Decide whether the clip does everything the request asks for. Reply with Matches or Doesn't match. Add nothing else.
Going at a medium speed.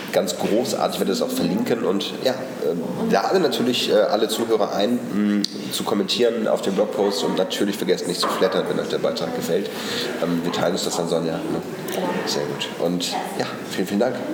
Matches